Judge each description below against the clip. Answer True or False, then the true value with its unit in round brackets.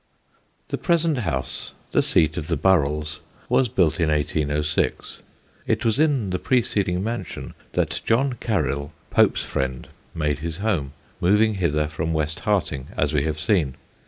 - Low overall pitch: True (80 Hz)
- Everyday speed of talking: True (150 wpm)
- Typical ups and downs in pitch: False (5.7 semitones)